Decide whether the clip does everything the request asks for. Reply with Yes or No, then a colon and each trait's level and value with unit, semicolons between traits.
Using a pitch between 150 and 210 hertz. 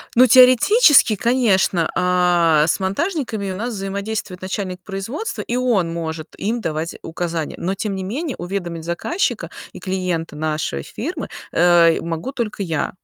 Yes: high, 190 Hz